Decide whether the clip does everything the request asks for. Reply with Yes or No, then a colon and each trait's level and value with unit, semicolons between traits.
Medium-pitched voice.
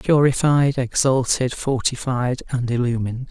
No: low, 130 Hz